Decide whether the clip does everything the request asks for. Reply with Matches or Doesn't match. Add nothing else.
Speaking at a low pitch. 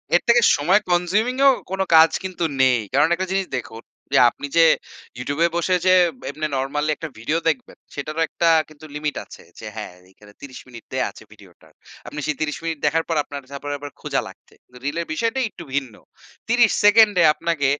Doesn't match